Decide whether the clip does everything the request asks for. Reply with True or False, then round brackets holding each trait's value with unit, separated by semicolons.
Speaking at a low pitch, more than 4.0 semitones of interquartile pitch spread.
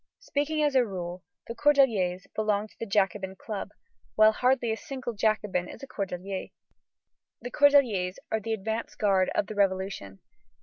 False (215 Hz; 4.4 semitones)